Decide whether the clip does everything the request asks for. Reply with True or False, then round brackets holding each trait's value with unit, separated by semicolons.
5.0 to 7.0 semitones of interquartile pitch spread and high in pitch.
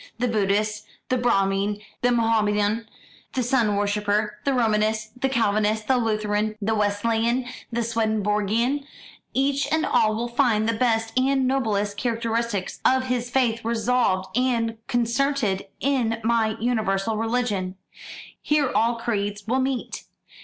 False (2.7 semitones; 225 Hz)